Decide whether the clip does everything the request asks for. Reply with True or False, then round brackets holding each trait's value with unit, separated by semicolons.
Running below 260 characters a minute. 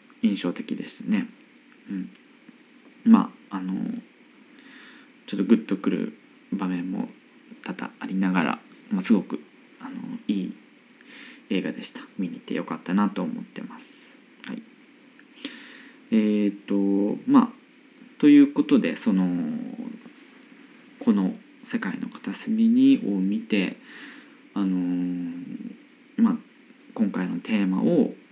True (210 characters per minute)